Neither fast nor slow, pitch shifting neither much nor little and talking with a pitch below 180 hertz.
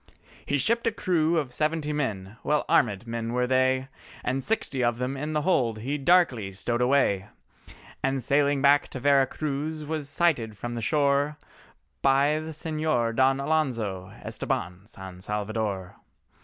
Yes: average, 150 wpm; average, 4.6 semitones; low, 135 Hz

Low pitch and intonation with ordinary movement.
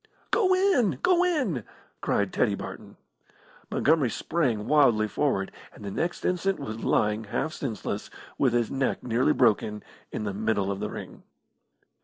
No: low, 125 Hz; wide, 8.1 semitones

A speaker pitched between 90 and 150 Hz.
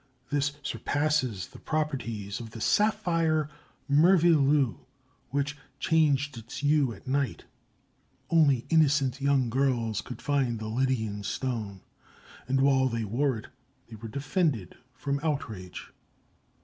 Yes: low, 135 Hz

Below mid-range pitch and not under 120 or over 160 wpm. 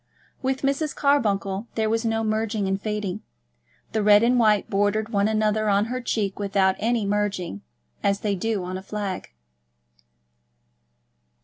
No: high, 210 Hz; average, 145 wpm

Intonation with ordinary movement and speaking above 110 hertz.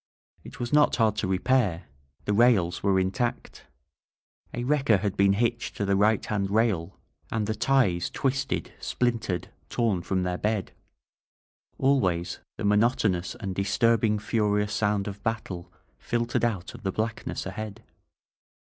No: average, 3.5 semitones; low, 105 Hz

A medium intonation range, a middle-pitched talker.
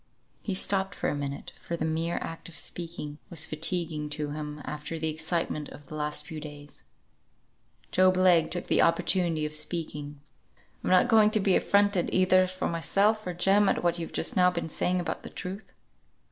Yes: average, 3.4 semitones; medium, 170 Hz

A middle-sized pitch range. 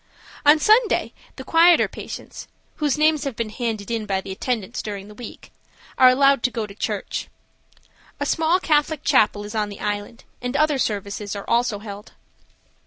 No: wide, 6.2 semitones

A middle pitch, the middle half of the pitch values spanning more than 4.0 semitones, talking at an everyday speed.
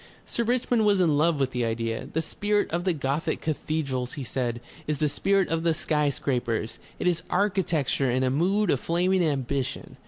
Yes: medium, 155 Hz; wide, 5.5 semitones; average, 190 wpm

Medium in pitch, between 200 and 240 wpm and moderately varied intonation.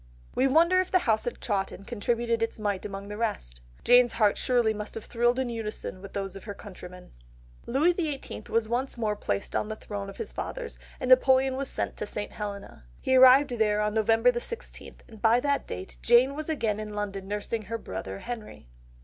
No: high, 225 Hz; fast, 205 wpm; average, 3.6 semitones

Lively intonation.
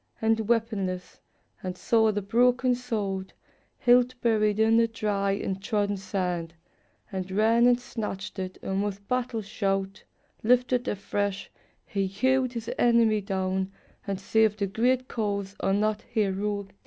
No: average, 3.1 semitones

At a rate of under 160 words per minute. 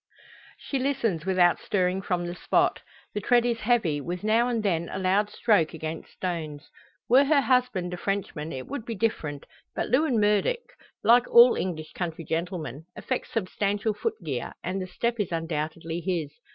No: average, 170 wpm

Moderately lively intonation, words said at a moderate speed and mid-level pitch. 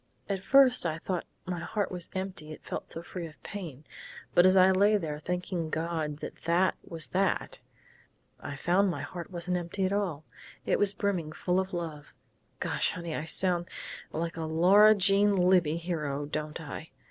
Yes: average, 3.0 semitones; average, 180 wpm; medium, 175 Hz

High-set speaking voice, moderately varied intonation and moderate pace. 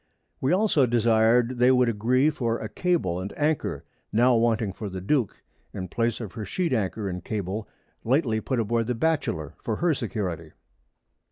No: low, 115 Hz; average, 3.8 semitones; average, 170 wpm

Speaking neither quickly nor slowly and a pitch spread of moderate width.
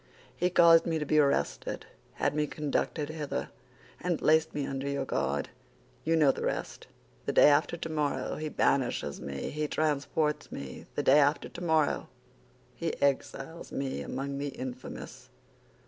No: average, 150 wpm; narrow, 2.3 semitones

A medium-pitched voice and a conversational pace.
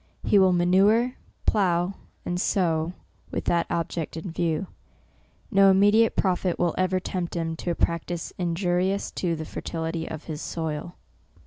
Yes: medium, 175 Hz; average, 150 wpm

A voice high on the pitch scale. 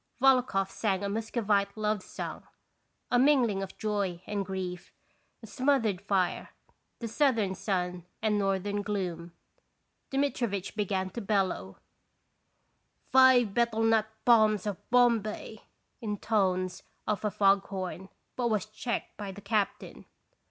Yes: high, 205 Hz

